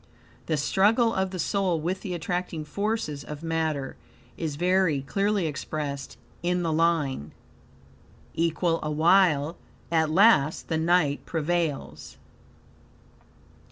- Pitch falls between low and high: Yes, medium, 165 Hz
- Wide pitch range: No, average, 3.2 semitones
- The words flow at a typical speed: No, slow, 110 wpm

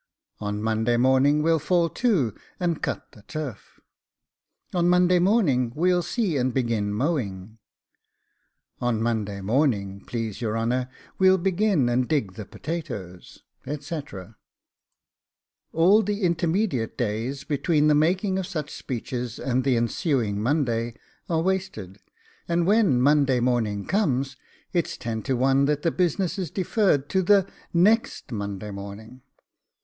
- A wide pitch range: Yes, wide, 7.2 semitones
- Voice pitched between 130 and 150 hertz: Yes, low, 135 Hz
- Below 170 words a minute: Yes, slow, 135 wpm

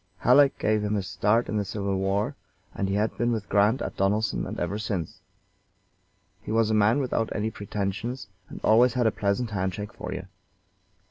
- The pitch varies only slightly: Yes, narrow, 2.3 semitones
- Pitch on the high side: No, low, 105 Hz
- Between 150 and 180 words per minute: No, average, 195 wpm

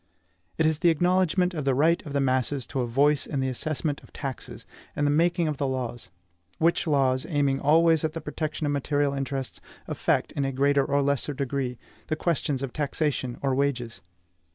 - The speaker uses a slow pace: No, average, 195 wpm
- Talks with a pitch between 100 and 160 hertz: Yes, medium, 140 Hz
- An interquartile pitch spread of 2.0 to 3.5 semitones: Yes, narrow, 2.6 semitones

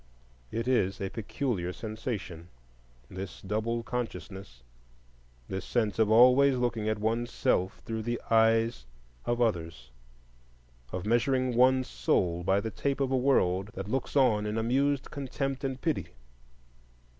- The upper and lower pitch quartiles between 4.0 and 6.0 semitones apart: Yes, average, 4.6 semitones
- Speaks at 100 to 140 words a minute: Yes, slow, 135 wpm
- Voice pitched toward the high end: No, low, 115 Hz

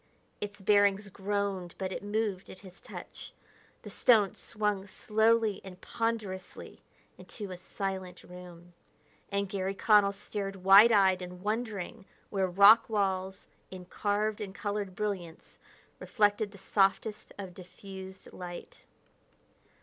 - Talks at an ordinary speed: No, slow, 125 wpm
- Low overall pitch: No, high, 200 Hz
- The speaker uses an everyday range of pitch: No, narrow, 1.8 semitones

